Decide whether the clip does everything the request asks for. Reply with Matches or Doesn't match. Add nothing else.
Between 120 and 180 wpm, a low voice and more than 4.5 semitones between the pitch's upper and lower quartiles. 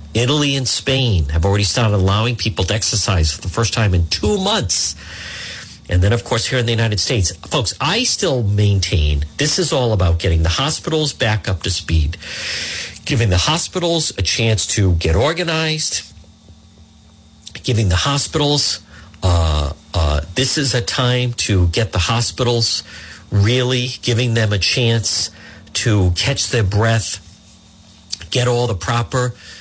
Matches